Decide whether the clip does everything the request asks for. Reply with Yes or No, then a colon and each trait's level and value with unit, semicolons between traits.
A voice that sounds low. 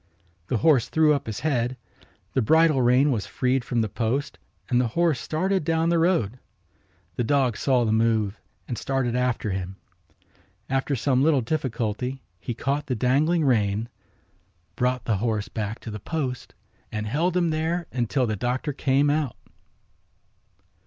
Yes: low, 130 Hz